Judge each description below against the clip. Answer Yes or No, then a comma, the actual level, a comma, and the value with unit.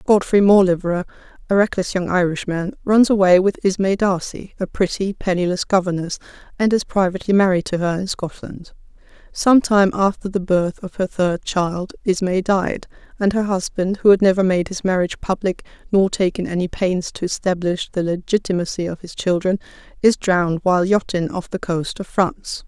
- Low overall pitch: No, medium, 185 Hz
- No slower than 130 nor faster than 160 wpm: No, average, 170 wpm